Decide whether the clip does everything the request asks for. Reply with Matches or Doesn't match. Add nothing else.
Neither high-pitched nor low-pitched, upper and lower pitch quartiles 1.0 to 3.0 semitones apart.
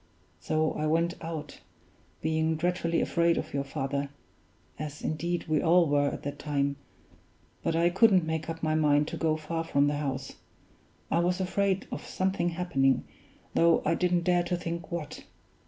Matches